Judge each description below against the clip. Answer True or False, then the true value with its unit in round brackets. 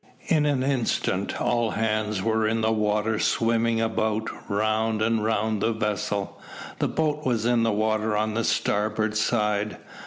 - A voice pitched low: True (110 Hz)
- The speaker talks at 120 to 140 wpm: False (155 wpm)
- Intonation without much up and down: True (1.2 semitones)